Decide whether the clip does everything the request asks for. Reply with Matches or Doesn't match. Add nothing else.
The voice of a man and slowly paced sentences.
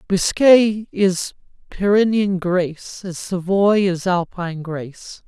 Matches